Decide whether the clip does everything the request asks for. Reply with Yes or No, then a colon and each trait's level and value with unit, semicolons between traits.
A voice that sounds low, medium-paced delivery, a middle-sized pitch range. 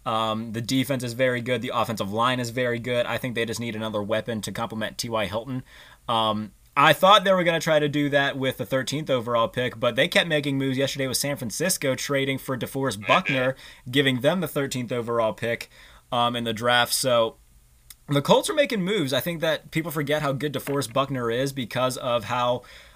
No: low, 130 Hz; fast, 210 wpm; average, 3.3 semitones